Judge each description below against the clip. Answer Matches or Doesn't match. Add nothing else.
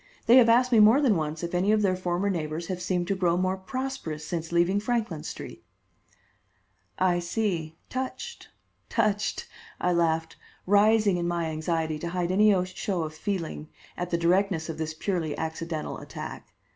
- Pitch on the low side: Doesn't match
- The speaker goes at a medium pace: Matches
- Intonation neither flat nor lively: Matches